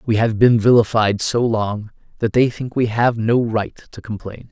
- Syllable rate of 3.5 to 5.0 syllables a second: Yes, 4.5 syllables/s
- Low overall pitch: Yes, low, 115 Hz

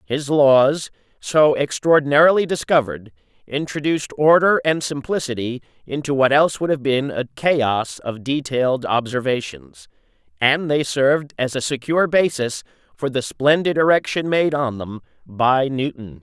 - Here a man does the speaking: Yes, male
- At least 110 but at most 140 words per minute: Yes, slow, 135 wpm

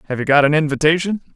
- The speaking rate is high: Yes, fast, 220 wpm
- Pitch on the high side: No, medium, 155 Hz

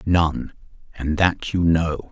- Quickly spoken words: No, average, 140 wpm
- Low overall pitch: Yes, very low, 80 Hz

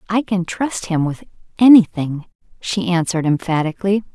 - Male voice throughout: No, female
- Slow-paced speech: Yes, slow, 130 wpm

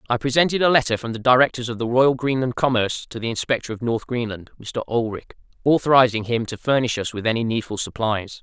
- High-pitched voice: No, low, 120 Hz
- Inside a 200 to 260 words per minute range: Yes, fast, 205 wpm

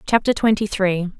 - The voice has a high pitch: Yes, high, 200 Hz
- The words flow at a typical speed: Yes, average, 150 wpm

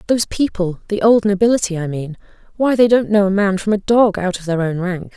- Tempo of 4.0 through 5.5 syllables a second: No, 5.8 syllables/s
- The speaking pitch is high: Yes, high, 200 Hz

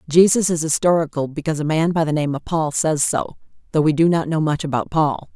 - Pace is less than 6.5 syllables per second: Yes, 5.9 syllables/s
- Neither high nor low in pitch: Yes, medium, 155 Hz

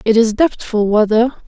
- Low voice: No, high, 225 Hz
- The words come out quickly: No, average, 160 wpm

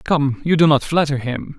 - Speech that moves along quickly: Yes, fast, 225 wpm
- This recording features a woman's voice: No, male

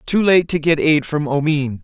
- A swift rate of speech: Yes, fast, 230 wpm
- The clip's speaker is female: No, male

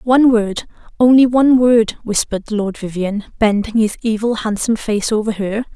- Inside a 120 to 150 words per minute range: Yes, average, 145 wpm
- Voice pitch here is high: Yes, high, 220 Hz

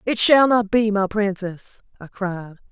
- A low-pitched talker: No, high, 205 Hz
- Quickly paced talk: No, average, 175 wpm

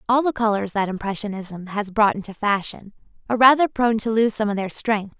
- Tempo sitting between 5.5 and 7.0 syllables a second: Yes, 5.8 syllables/s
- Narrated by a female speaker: Yes, female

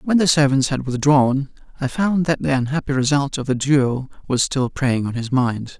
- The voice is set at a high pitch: No, low, 135 Hz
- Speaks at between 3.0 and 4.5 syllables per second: No, 4.7 syllables/s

